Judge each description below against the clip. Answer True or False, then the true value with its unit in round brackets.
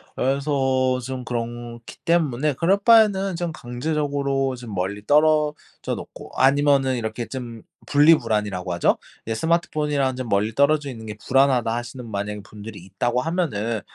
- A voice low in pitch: True (130 Hz)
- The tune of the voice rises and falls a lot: False (4.6 semitones)